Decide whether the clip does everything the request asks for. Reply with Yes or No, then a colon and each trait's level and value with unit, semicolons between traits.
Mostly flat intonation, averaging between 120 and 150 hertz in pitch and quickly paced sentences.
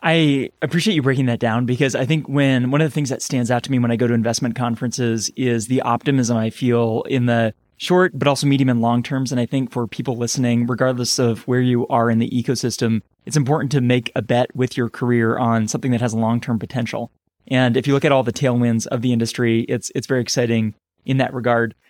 Yes: narrow, 2.3 semitones; low, 125 Hz; fast, 240 wpm